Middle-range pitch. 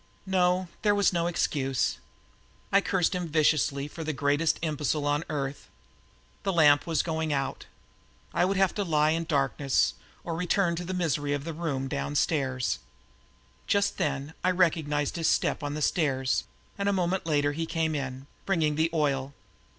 Yes: medium, 155 Hz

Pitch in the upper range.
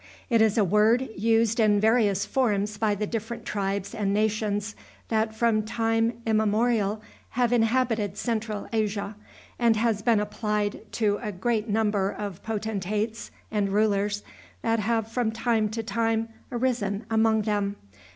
Yes: high, 220 Hz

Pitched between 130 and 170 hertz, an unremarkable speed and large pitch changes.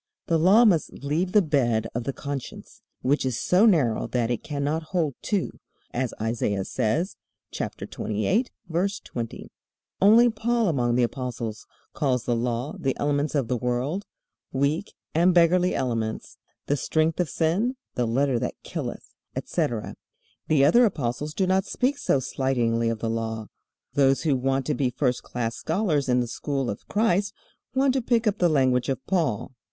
Yes: medium, 140 Hz; average, 170 wpm; wide, 6.7 semitones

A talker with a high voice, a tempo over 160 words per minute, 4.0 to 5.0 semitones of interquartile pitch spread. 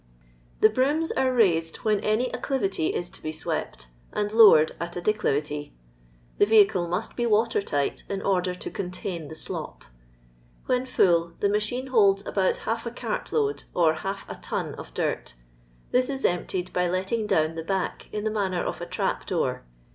Yes: high, 195 Hz; average, 180 wpm; average, 4.5 semitones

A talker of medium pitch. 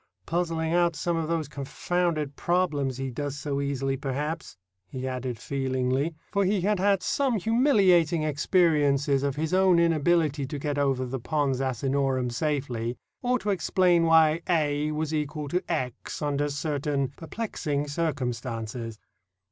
Yes: medium, 150 Hz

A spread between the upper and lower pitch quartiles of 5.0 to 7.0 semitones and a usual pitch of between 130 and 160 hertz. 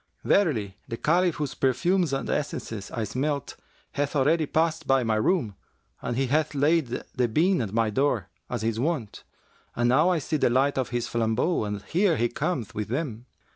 Yes: average, 5.3 semitones; low, 135 Hz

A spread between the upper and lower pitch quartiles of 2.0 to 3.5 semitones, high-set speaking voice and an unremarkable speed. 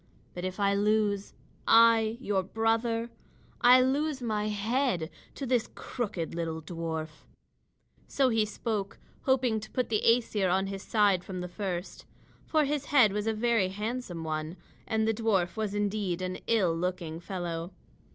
No: average, 4.0 semitones; high, 210 Hz; average, 155 wpm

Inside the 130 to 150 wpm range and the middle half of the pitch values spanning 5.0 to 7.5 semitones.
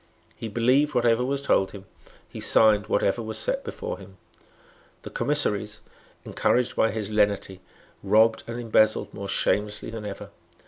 No: average, 145 wpm; average, 2.8 semitones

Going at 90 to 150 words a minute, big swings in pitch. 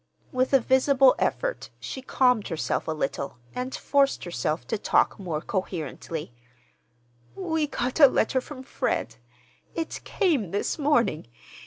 Yes: slow, 135 wpm; wide, 8.3 semitones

